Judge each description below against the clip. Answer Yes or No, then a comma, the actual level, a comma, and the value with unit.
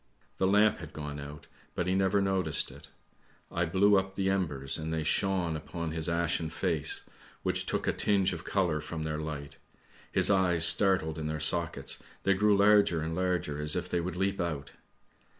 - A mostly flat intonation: No, average, 3.6 semitones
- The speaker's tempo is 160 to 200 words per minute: Yes, average, 185 wpm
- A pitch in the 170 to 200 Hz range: No, very low, 85 Hz